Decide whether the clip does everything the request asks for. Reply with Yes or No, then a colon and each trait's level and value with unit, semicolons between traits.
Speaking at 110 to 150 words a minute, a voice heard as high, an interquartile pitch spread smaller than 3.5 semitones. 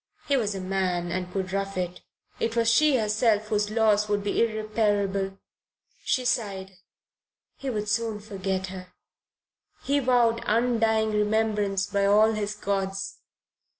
Yes: average, 140 wpm; high, 210 Hz; narrow, 2.4 semitones